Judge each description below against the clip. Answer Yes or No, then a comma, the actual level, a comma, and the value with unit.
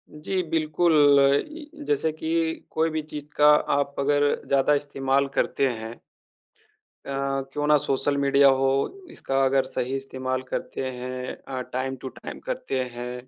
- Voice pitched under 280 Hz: Yes, medium, 140 Hz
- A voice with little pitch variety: Yes, narrow, 2.1 semitones